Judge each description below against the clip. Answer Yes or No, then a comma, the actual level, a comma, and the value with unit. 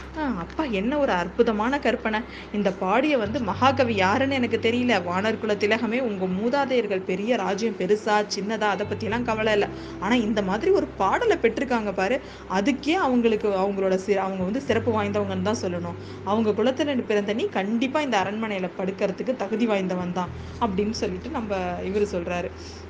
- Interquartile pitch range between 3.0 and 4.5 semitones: Yes, average, 3.8 semitones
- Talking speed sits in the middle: No, fast, 150 wpm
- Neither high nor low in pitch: No, high, 215 Hz